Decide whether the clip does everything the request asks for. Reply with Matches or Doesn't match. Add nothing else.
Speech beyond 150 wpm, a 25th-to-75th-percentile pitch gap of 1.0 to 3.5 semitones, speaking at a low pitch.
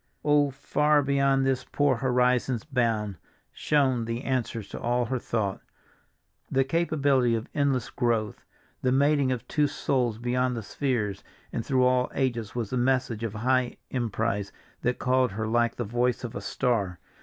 Matches